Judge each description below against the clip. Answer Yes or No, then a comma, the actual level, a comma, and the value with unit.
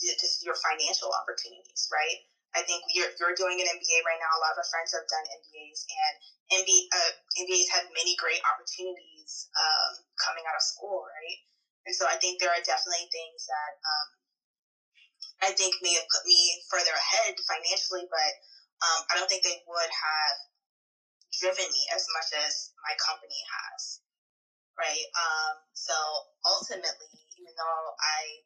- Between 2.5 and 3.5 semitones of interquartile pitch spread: Yes, average, 2.9 semitones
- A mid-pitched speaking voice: Yes, medium, 175 Hz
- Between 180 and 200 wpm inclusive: No, average, 165 wpm